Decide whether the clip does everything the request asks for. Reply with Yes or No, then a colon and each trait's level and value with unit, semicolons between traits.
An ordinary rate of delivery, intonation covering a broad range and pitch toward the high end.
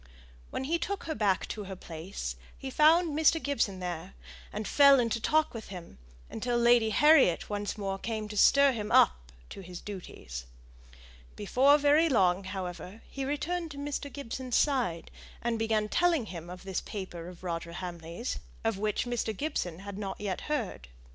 Yes: average, 170 wpm; wide, 7.3 semitones; high, 215 Hz